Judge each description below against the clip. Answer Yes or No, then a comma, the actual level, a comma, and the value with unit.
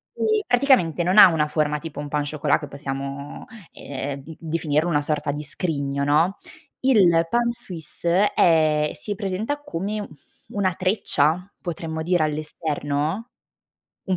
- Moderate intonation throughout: Yes, average, 4.3 semitones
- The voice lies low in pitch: No, medium, 160 Hz